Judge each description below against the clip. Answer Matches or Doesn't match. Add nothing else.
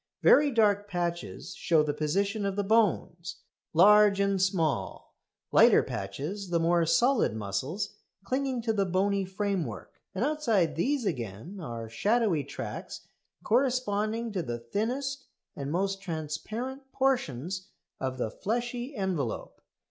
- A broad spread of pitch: Matches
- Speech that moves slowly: Matches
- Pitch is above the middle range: Matches